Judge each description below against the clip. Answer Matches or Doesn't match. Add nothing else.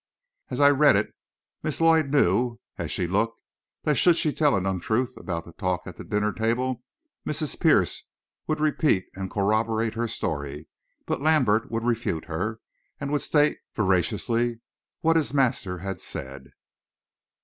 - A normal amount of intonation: Doesn't match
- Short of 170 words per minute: Matches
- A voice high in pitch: Doesn't match